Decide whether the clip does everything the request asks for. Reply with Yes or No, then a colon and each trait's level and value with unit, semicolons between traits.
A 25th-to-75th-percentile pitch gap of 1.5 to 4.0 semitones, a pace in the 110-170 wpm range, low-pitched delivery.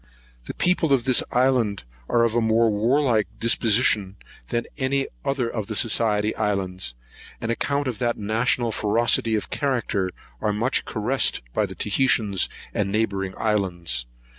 Yes: average, 3.2 semitones; average, 150 wpm; low, 115 Hz